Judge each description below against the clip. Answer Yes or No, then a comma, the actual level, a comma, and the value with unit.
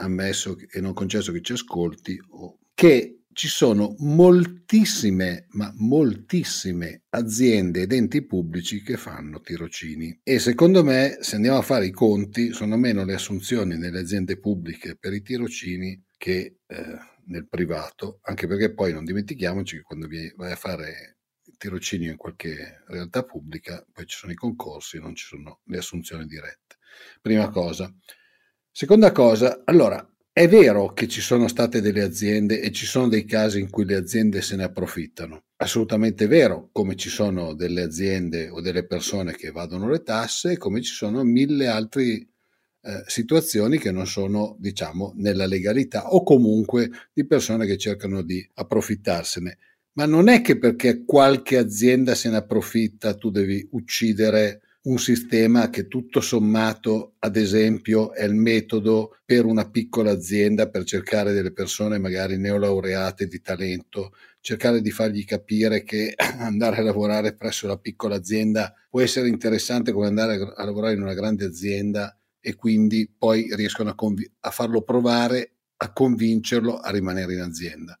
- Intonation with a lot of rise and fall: No, average, 3.6 semitones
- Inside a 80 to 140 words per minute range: No, average, 155 wpm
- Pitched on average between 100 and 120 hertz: Yes, low, 105 Hz